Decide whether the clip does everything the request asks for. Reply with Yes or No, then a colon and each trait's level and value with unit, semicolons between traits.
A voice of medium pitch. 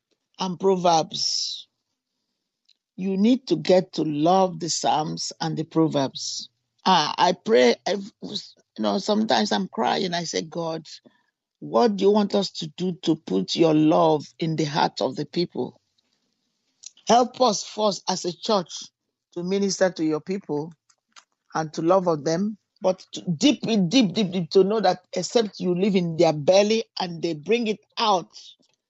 Yes: medium, 180 Hz